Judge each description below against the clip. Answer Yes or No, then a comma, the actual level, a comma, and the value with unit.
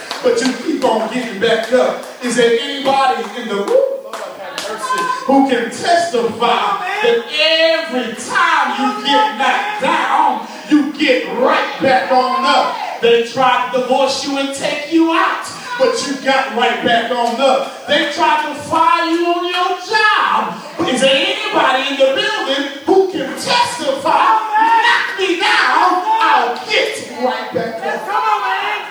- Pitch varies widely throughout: Yes, wide, 6.2 semitones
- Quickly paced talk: No, average, 150 wpm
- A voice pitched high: Yes, very high, 275 Hz